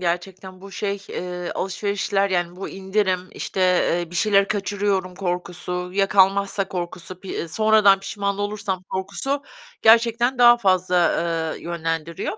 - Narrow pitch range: Yes, narrow, 2.1 semitones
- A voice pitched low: No, high, 195 Hz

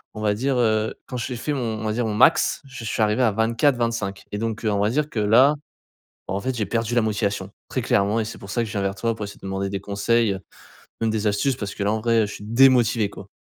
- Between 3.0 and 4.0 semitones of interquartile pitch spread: No, narrow, 2.6 semitones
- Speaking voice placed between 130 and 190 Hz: No, low, 110 Hz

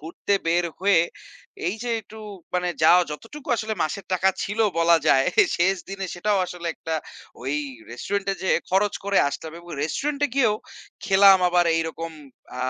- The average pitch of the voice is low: No, high, 190 Hz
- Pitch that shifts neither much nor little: Yes, average, 3.3 semitones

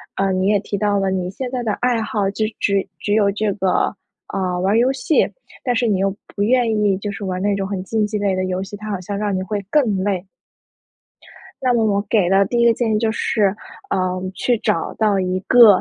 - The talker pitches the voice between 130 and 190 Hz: No, high, 205 Hz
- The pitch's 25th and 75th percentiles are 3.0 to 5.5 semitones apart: No, narrow, 2.4 semitones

